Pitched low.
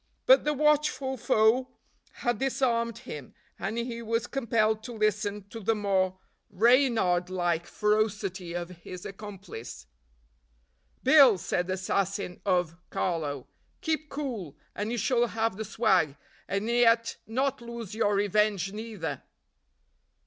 No: high, 215 Hz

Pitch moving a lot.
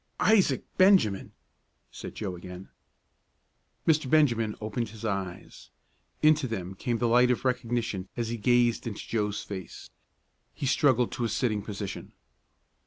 No: average, 3.4 semitones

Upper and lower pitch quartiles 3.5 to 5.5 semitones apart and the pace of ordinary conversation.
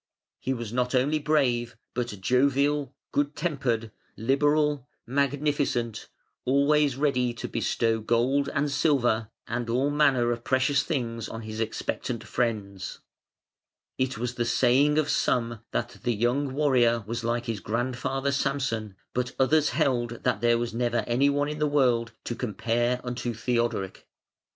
No: average, 3.1 semitones; average, 145 wpm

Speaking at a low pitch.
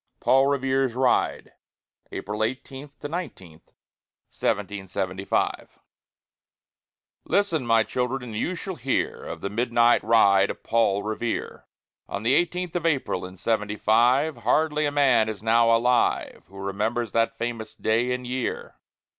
Yes: low, 120 Hz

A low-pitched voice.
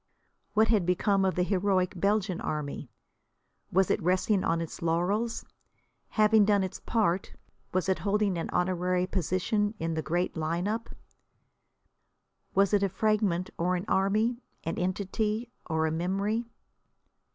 No: high, 190 Hz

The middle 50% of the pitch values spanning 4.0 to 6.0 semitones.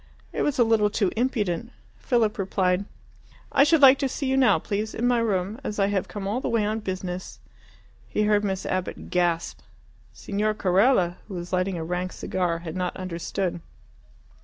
No: average, 3.6 semitones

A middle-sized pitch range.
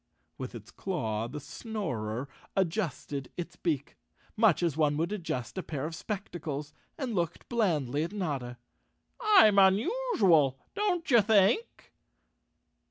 No: wide, 6.9 semitones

